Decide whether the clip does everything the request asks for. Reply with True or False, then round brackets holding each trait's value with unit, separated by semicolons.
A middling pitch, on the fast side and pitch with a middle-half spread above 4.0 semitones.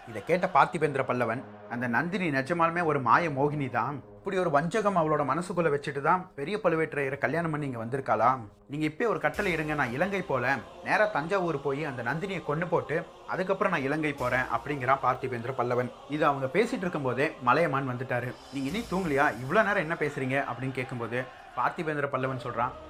True (145 Hz; 145 wpm; 4.4 semitones)